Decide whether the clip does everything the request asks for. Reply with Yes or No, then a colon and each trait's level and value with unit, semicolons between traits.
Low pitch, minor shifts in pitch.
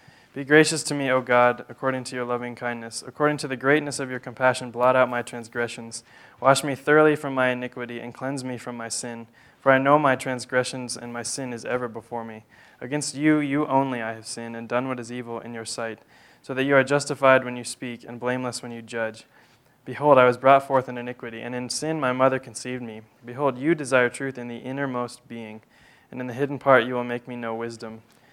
Yes: low, 125 Hz; narrow, 2.2 semitones